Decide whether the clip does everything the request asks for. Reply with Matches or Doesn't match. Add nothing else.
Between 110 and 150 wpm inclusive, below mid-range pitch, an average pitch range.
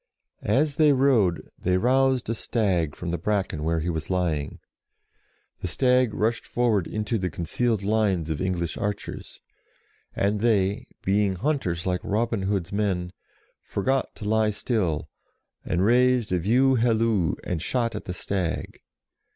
Matches